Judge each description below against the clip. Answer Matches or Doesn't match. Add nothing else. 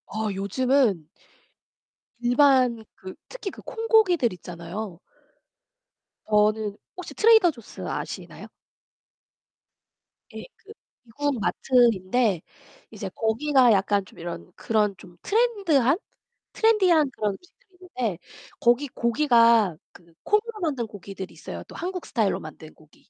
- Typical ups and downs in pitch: Doesn't match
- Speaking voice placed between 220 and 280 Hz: Matches